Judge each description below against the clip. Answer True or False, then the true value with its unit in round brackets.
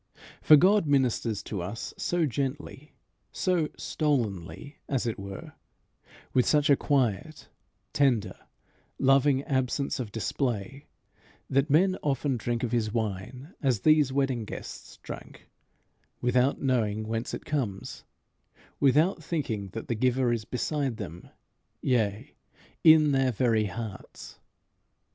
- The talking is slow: True (120 wpm)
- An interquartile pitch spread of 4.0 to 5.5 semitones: True (4.4 semitones)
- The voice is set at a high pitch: False (130 Hz)